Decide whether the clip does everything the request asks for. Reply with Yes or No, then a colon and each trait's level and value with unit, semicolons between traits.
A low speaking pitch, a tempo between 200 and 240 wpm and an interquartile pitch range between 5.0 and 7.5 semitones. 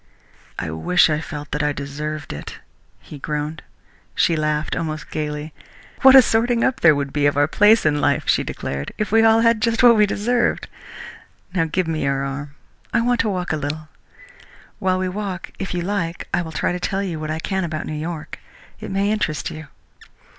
No: medium, 160 Hz; fast, 205 wpm; average, 5.3 semitones